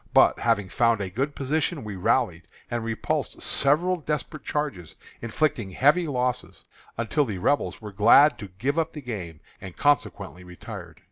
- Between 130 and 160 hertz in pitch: No, low, 120 Hz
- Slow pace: No, average, 155 wpm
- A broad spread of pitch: Yes, wide, 6.3 semitones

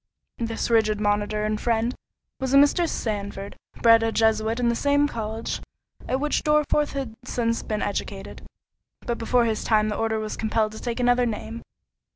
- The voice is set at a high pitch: Yes, high, 225 Hz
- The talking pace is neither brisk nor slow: Yes, average, 175 wpm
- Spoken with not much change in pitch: Yes, narrow, 2.3 semitones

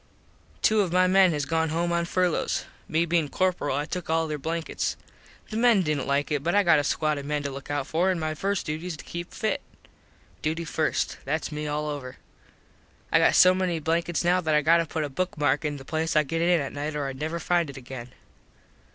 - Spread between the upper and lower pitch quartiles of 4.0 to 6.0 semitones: No, average, 2.8 semitones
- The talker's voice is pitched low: No, medium, 160 Hz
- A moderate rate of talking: No, fast, 240 wpm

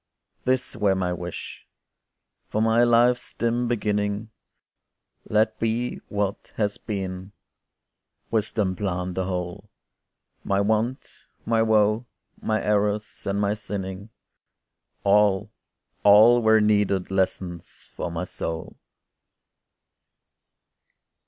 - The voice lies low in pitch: Yes, low, 105 Hz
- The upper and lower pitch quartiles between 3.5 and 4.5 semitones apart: No, narrow, 2.5 semitones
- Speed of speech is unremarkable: No, slow, 95 wpm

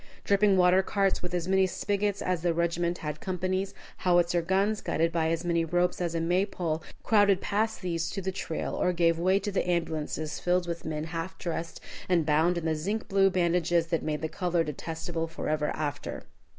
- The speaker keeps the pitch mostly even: Yes, narrow, 2.3 semitones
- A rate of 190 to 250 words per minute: Yes, average, 195 wpm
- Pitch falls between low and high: Yes, medium, 175 Hz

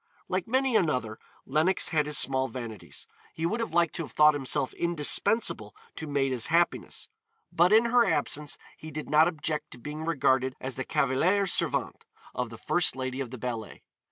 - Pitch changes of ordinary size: Yes, average, 4.6 semitones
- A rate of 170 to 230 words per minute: Yes, average, 180 wpm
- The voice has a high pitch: No, medium, 150 Hz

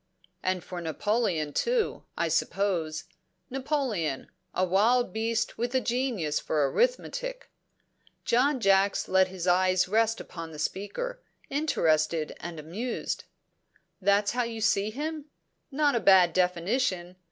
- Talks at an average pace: No, slow, 125 wpm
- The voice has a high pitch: Yes, high, 200 Hz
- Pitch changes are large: Yes, wide, 6.1 semitones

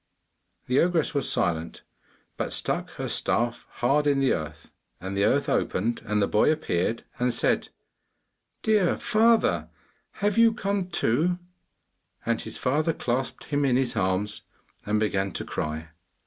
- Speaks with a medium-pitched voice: No, low, 125 Hz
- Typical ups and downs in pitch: No, wide, 8.0 semitones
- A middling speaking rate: Yes, average, 150 wpm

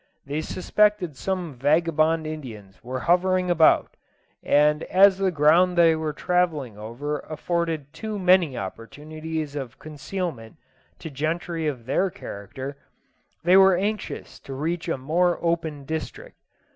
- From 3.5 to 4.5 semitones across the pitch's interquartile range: Yes, average, 3.8 semitones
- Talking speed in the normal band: No, slow, 130 wpm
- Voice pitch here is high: No, medium, 160 Hz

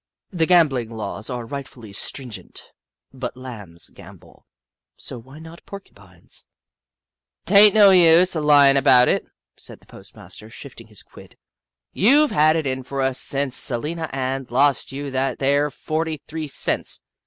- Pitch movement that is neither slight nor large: Yes, average, 4.1 semitones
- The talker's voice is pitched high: No, medium, 140 Hz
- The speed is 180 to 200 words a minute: No, average, 165 wpm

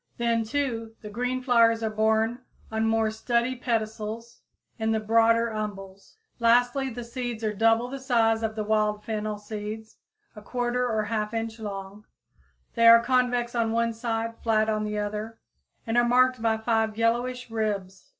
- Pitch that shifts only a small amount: Yes, narrow, 1.6 semitones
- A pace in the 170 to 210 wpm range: No, average, 160 wpm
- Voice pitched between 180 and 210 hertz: No, high, 225 Hz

